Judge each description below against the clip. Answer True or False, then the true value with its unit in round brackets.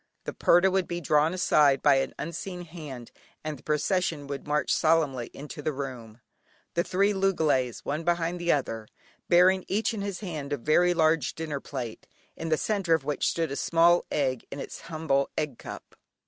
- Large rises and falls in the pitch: False (3.8 semitones)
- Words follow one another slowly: False (185 wpm)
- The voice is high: False (155 Hz)